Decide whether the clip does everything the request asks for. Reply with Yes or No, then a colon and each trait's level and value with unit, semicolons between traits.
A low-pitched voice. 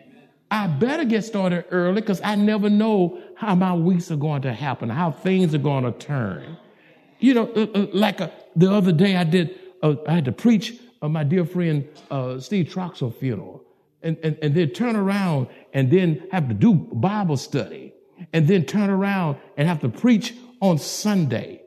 No: medium, 180 Hz